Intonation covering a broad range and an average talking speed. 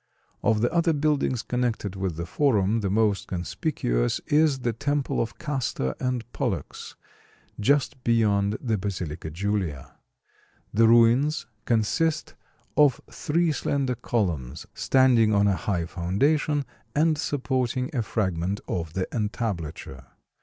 No: wide, 6.1 semitones; slow, 125 wpm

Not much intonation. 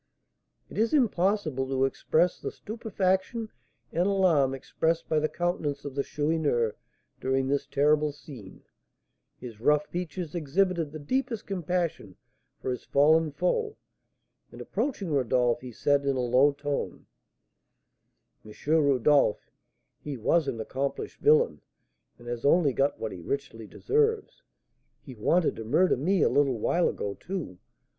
No: average, 5.3 semitones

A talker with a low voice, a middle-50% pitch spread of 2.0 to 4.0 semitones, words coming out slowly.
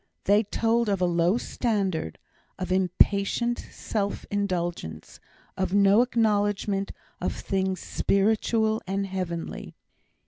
No: high, 200 Hz; narrow, 2.5 semitones; slow, 105 wpm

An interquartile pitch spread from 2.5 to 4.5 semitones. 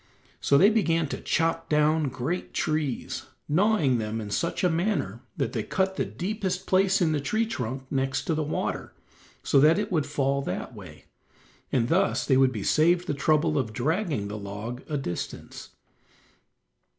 No: average, 5.3 semitones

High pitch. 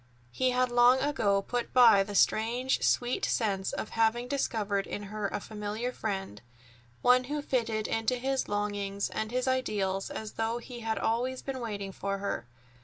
Yes: high, 220 Hz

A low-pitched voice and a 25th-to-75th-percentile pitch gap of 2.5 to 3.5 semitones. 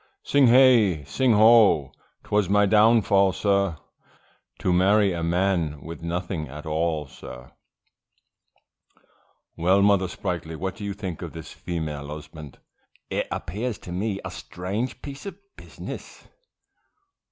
No: very low, 95 Hz; average, 4.2 semitones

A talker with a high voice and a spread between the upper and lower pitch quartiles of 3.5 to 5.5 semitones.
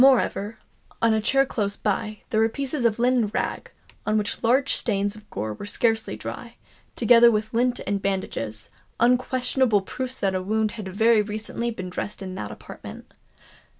No: high, 220 Hz; average, 2.9 semitones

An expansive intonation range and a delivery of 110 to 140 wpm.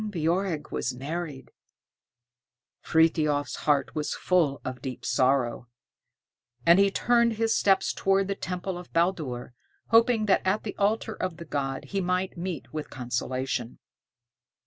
Yes: wide, 5.9 semitones; slow, 135 wpm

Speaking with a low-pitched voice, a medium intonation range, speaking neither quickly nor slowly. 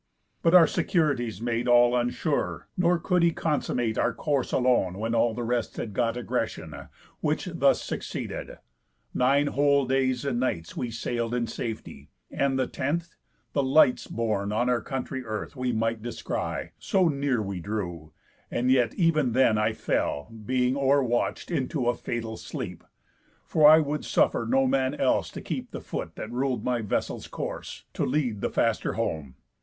Yes: low, 125 Hz; average, 3.4 semitones; average, 165 wpm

